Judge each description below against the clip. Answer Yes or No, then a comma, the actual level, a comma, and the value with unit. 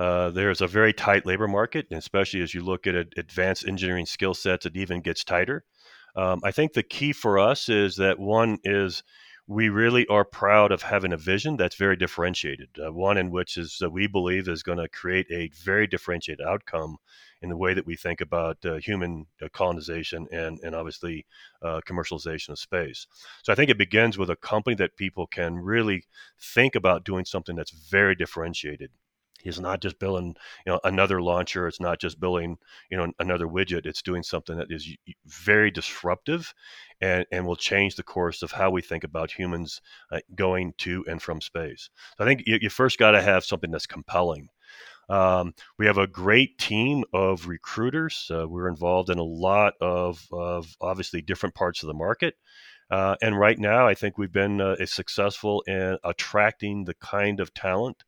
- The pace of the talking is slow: No, average, 195 wpm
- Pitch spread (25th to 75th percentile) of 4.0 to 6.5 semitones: No, average, 2.7 semitones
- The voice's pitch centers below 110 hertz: Yes, very low, 90 Hz